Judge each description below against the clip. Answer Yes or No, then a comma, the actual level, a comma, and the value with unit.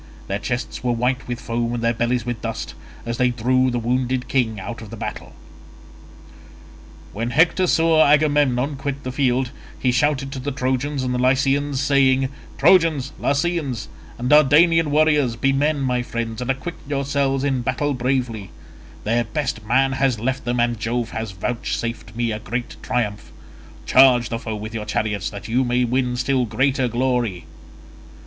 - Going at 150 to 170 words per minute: Yes, average, 165 wpm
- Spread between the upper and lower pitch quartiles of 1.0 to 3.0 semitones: Yes, average, 2.7 semitones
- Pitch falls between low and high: No, low, 125 Hz